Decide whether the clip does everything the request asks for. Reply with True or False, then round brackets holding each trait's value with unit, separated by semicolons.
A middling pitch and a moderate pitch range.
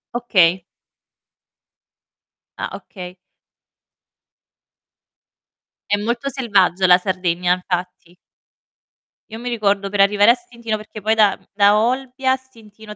False (210 Hz; 4.1 semitones)